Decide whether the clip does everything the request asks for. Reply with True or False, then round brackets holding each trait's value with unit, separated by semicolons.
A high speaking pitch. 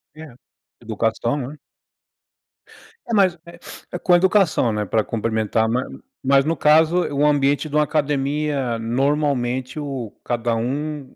False (140 Hz)